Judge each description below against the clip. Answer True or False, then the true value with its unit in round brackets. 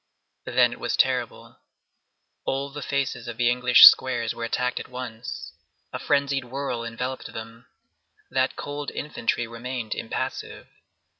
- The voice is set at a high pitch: False (125 Hz)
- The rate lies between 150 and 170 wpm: False (135 wpm)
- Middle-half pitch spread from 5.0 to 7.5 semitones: False (2.6 semitones)